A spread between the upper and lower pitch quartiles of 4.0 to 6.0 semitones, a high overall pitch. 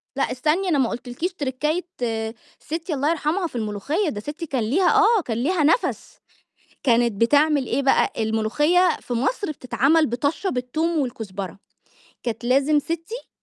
Yes: wide, 5.4 semitones; very high, 285 Hz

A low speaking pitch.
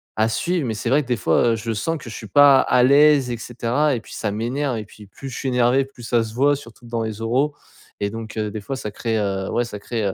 Yes: low, 120 Hz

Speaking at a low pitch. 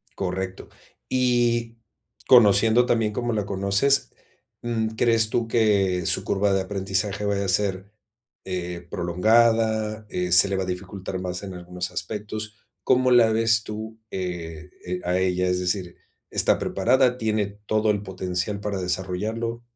Yes: low, 100 Hz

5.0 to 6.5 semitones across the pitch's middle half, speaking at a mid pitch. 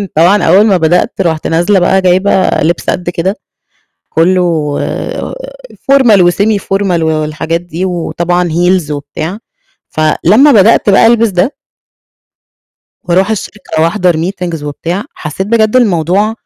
No: average, 3.4 semitones; medium, 180 Hz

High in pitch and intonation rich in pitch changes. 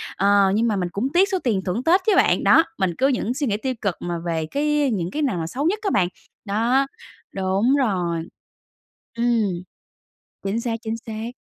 Yes: high, 225 Hz; wide, 5.9 semitones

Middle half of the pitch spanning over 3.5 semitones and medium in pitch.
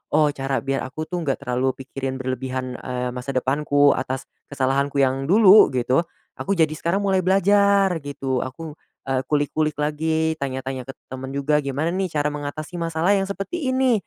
Yes: average, 4.2 semitones; medium, 145 Hz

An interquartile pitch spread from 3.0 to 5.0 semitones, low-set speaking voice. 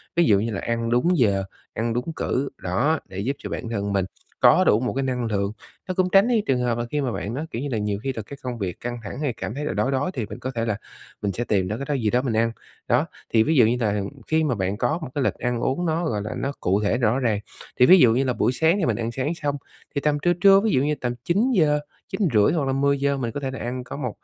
Yes: average, 4.6 semitones; low, 125 Hz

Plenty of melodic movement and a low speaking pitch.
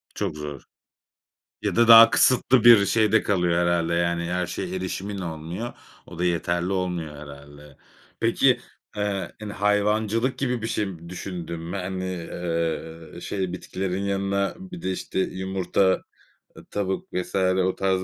No: average, 3.1 semitones; very low, 95 Hz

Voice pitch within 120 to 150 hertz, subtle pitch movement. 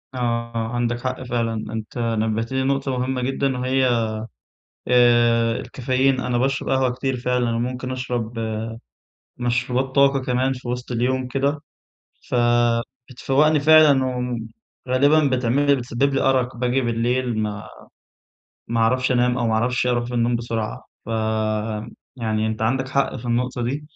Yes: low, 125 Hz; narrow, 2.0 semitones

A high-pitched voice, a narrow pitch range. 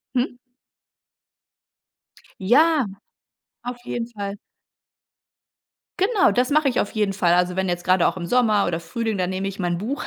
No: high, 205 Hz; average, 5.1 semitones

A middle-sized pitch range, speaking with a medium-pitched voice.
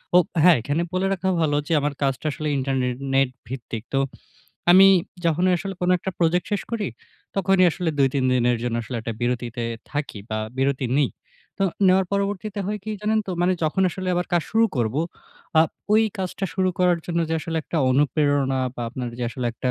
No: wide, 6.1 semitones; medium, 155 Hz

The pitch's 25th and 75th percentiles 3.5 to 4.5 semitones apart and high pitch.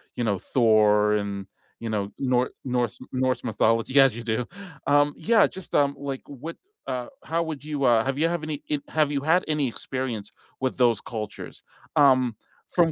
No: average, 4.2 semitones; low, 130 Hz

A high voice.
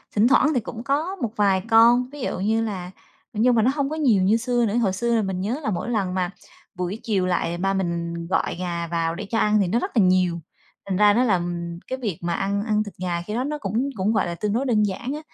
Yes: high, 210 Hz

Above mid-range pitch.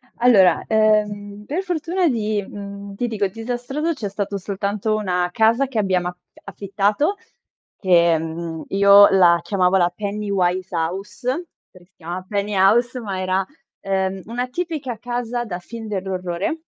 Yes: high, 200 Hz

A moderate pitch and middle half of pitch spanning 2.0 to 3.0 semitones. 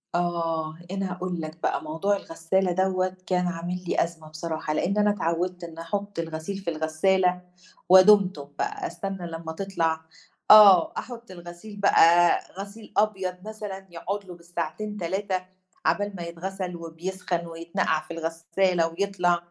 Yes: medium, 180 Hz; narrow, 2.6 semitones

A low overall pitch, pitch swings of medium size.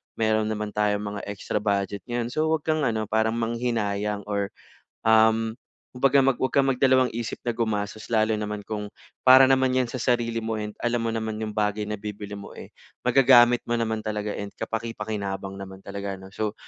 No: low, 110 Hz; narrow, 2.3 semitones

